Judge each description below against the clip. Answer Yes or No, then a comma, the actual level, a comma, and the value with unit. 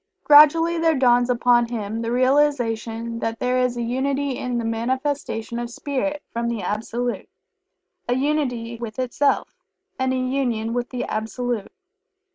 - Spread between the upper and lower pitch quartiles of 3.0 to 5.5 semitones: No, narrow, 2.6 semitones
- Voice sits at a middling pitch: No, high, 245 Hz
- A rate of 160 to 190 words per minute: No, average, 145 wpm